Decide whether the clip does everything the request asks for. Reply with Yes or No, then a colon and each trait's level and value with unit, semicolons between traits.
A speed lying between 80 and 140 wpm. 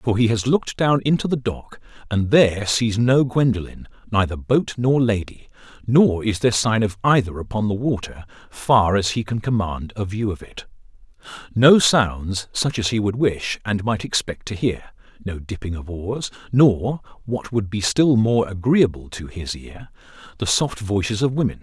No: average, 175 wpm